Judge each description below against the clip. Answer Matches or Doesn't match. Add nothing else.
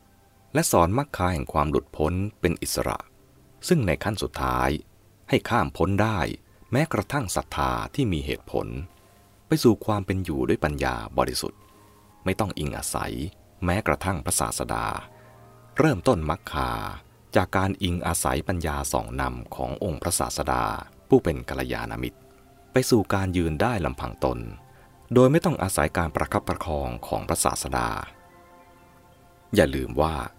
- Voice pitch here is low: Matches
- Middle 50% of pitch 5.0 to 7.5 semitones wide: Matches